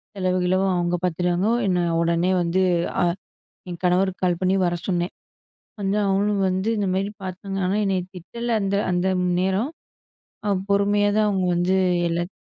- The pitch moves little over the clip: Yes, narrow, 1.8 semitones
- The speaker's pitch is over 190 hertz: No, medium, 185 Hz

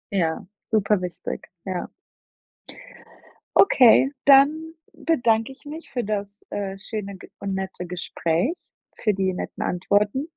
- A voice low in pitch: No, high, 210 Hz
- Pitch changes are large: Yes, wide, 5.9 semitones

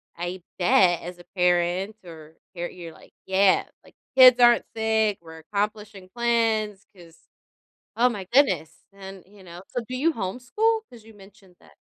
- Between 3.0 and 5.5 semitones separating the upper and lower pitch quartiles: Yes, average, 4.2 semitones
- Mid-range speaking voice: No, high, 195 Hz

